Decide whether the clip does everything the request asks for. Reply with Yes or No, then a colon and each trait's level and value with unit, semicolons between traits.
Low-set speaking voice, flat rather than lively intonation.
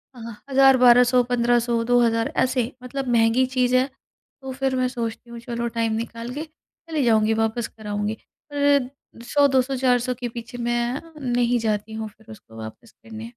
No: high, 240 Hz; narrow, 2.1 semitones